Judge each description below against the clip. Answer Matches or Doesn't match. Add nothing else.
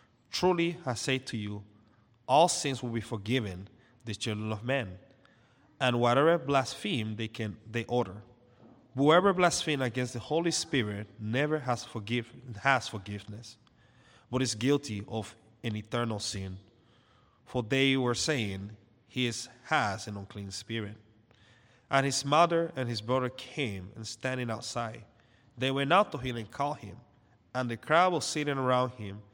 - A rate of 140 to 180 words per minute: Matches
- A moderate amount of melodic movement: Matches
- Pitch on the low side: Matches